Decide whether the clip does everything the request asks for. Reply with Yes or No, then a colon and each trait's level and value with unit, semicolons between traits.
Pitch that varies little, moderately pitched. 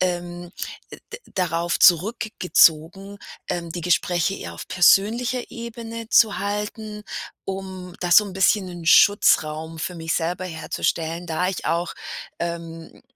No: average, 3.2 semitones; medium, 180 Hz